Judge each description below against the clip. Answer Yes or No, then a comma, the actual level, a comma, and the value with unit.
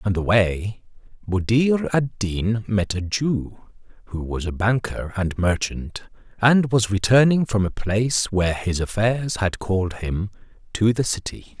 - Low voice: Yes, low, 105 Hz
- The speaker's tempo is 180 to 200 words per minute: No, average, 155 wpm